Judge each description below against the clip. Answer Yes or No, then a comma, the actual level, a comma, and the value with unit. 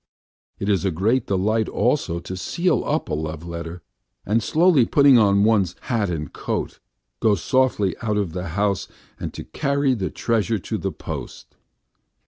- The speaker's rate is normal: Yes, average, 170 wpm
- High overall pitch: No, low, 105 Hz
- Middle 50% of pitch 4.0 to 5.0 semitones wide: Yes, average, 4.7 semitones